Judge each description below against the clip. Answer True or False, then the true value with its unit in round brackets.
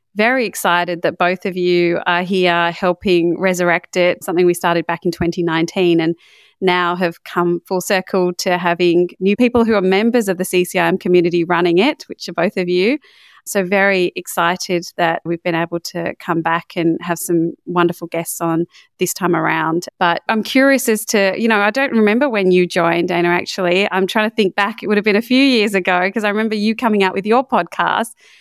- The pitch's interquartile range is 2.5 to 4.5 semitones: True (3.0 semitones)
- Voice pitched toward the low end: False (180 Hz)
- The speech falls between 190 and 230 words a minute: True (205 wpm)